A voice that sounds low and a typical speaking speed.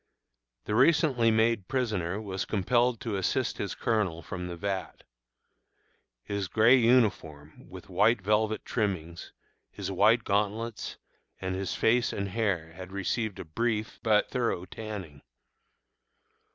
No: low, 105 Hz; slow, 125 wpm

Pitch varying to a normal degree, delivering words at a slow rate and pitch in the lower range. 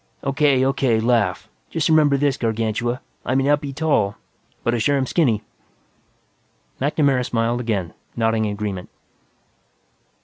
Yes: average, 4.0 semitones; slow, 130 wpm; low, 125 Hz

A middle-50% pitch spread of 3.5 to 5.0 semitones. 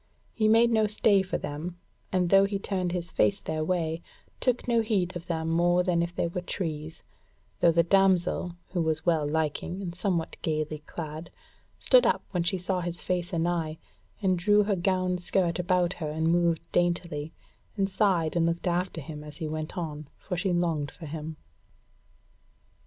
No: narrow, 2.6 semitones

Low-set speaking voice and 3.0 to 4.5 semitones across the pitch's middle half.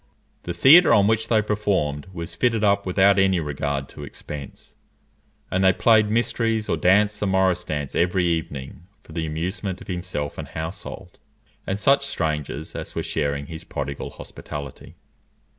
No: very low, 90 Hz; average, 5.2 semitones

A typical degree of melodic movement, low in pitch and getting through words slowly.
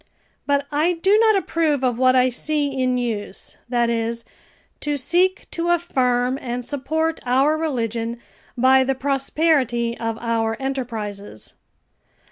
No: average, 4.3 semitones; very high, 260 Hz; slow, 130 wpm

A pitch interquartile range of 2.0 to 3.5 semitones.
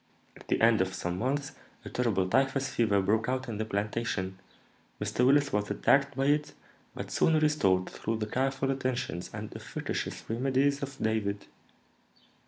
No: average, 4.8 semitones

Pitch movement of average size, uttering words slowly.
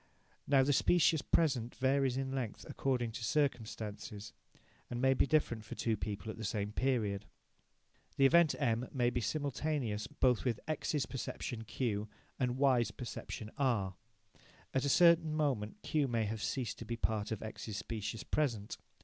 No: average, 3.9 semitones; average, 160 wpm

